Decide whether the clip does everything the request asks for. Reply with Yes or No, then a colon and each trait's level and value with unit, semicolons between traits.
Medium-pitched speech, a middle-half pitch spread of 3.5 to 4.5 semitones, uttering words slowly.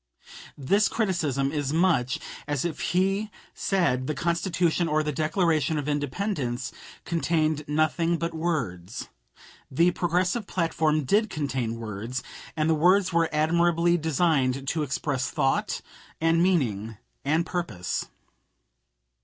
Yes: medium, 155 Hz; average, 4.1 semitones; slow, 120 wpm